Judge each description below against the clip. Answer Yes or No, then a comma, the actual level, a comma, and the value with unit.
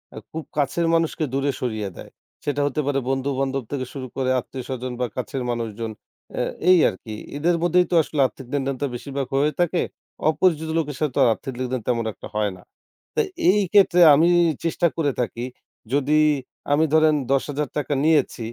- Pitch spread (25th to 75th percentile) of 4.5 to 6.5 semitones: No, average, 3.5 semitones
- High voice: No, medium, 140 Hz